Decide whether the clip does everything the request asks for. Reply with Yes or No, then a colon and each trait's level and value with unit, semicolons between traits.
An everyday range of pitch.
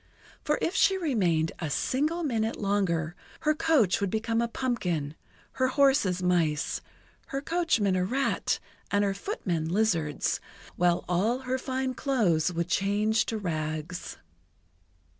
No: wide, 7.0 semitones